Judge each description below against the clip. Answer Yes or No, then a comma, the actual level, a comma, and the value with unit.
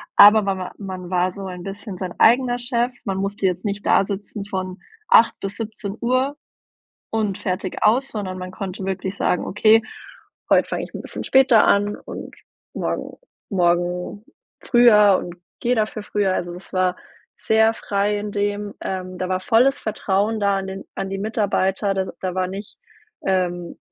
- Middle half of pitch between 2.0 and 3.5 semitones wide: Yes, narrow, 2.5 semitones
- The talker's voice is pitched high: Yes, high, 200 Hz